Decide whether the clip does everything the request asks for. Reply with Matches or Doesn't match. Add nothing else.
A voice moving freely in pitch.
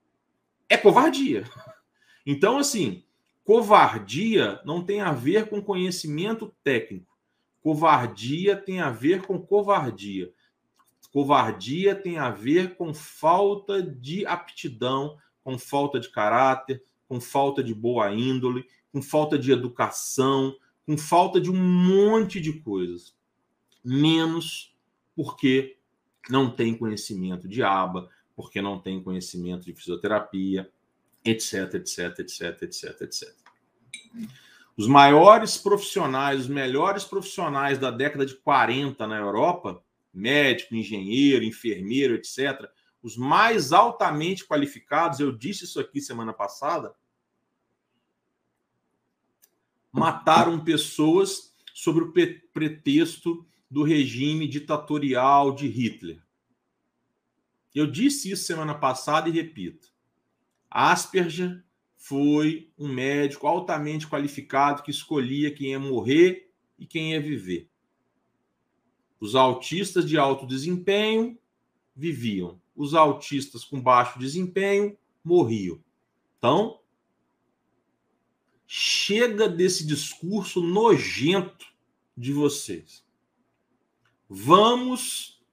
Matches